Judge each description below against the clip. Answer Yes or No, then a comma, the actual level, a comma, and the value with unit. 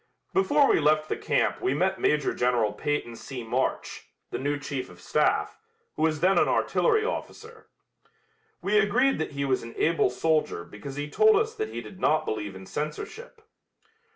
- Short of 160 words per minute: No, average, 180 wpm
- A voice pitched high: No, medium, 155 Hz